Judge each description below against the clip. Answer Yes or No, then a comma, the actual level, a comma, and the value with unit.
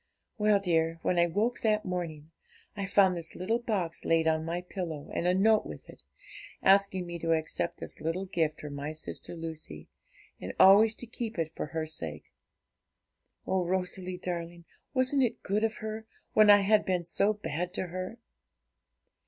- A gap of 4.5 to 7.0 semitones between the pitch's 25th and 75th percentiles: No, average, 3.9 semitones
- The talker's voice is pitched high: No, medium, 180 Hz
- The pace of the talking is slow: No, average, 175 wpm